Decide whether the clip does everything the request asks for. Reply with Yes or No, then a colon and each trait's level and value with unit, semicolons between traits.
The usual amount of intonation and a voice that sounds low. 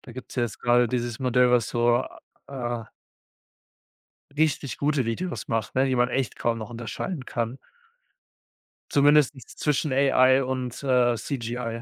No: narrow, 2.2 semitones; low, 125 Hz